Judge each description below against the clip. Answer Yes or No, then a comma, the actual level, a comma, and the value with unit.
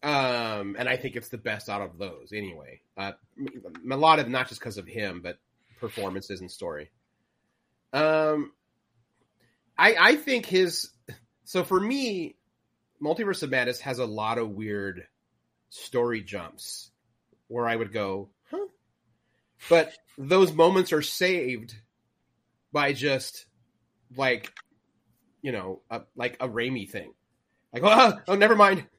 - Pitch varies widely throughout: Yes, wide, 6.2 semitones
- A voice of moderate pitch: No, low, 120 Hz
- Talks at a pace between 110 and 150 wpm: Yes, average, 140 wpm